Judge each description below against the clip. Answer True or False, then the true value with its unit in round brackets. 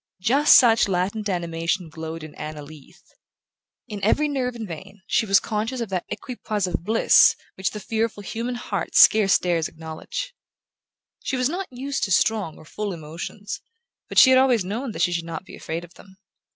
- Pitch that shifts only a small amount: False (5.4 semitones)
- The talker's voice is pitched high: True (200 Hz)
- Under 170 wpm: False (190 wpm)